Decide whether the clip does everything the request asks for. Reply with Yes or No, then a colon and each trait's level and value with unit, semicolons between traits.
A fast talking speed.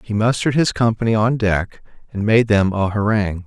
No: average, 190 wpm